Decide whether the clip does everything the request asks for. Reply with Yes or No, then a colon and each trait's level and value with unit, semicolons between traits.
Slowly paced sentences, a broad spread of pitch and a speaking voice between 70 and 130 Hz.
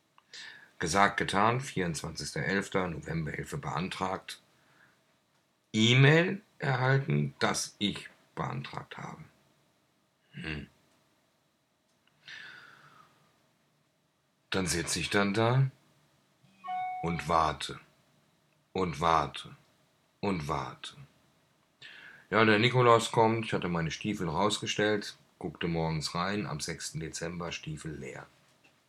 Yes: slow, 85 wpm; wide, 7.2 semitones; low, 110 Hz